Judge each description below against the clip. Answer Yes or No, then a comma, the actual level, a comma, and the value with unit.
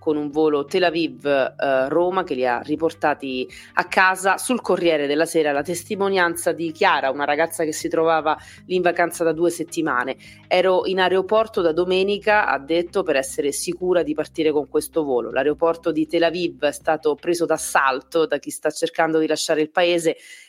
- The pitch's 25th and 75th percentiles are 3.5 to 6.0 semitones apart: No, narrow, 2.6 semitones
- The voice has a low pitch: No, medium, 165 Hz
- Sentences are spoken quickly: Yes, fast, 180 wpm